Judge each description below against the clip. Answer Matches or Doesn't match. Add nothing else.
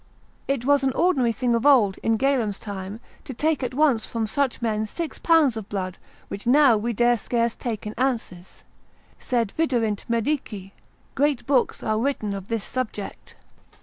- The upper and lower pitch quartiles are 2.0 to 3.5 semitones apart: Doesn't match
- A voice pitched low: Doesn't match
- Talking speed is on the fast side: Doesn't match